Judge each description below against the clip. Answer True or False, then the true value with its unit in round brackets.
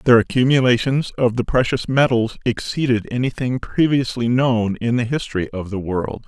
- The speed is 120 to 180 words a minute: True (155 wpm)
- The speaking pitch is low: True (120 Hz)